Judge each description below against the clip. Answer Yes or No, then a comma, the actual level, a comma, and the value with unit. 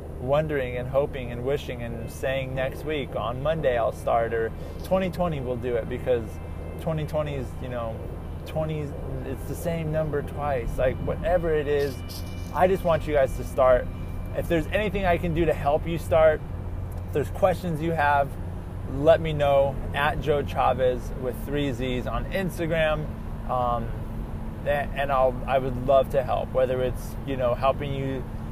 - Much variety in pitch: Yes, wide, 5.7 semitones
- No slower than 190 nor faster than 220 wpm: No, average, 170 wpm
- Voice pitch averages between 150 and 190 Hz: No, low, 130 Hz